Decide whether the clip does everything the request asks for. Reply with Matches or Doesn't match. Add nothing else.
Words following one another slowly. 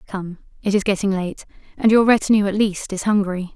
Doesn't match